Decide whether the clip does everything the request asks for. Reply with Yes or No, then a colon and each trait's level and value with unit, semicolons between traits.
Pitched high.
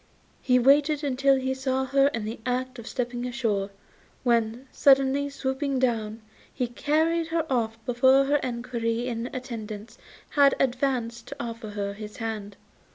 Yes: very high, 250 Hz